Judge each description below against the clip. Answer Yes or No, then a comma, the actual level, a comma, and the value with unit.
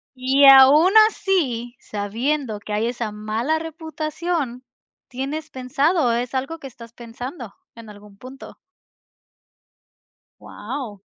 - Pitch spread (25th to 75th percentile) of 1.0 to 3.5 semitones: No, average, 4.7 semitones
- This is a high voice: Yes, very high, 255 Hz